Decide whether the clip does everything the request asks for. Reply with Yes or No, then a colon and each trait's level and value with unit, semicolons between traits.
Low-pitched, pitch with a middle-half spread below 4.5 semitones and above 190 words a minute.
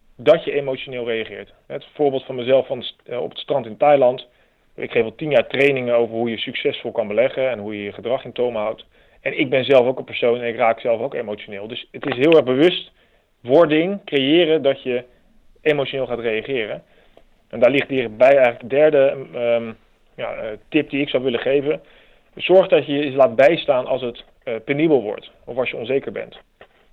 Yes: low, 130 Hz; average, 3.5 semitones; fast, 200 wpm